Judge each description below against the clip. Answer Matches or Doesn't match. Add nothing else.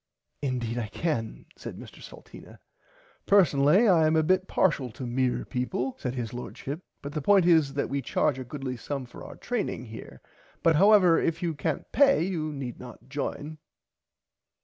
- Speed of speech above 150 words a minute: Matches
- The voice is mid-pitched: Matches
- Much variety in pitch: Doesn't match